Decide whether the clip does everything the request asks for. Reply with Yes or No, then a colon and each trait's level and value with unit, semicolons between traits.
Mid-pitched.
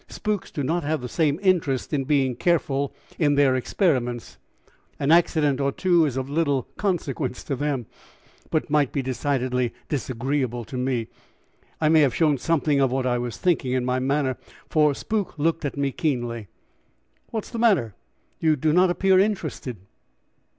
Yes: medium, 145 Hz